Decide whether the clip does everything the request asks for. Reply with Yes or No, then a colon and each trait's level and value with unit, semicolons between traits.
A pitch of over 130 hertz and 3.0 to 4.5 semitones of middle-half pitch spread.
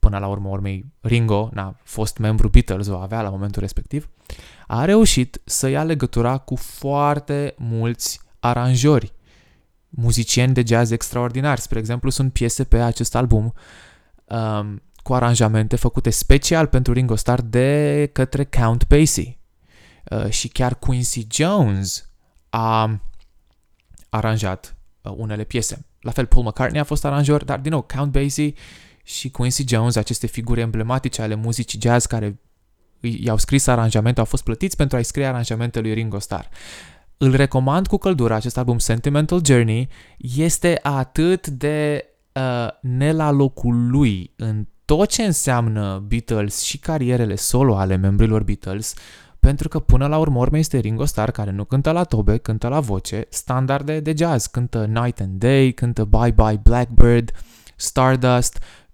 No: low, 120 Hz; average, 3.8 semitones